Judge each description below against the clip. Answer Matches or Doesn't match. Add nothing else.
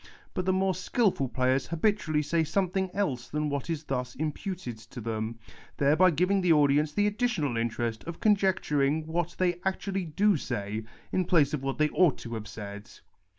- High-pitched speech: Doesn't match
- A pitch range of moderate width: Doesn't match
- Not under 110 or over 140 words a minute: Doesn't match